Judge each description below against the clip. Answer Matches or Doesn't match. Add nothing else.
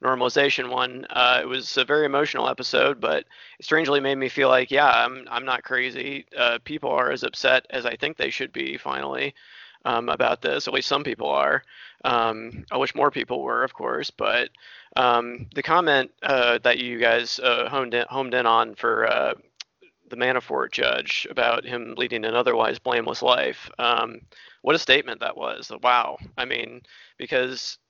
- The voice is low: Matches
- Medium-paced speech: Matches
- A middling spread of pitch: Doesn't match